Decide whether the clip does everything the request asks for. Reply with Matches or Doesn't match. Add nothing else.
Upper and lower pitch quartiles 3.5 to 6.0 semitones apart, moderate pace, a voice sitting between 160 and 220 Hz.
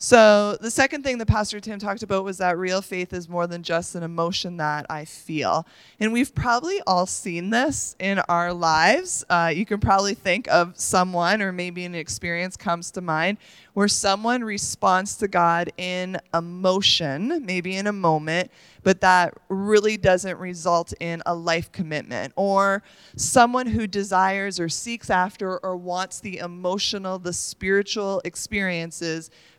Doesn't match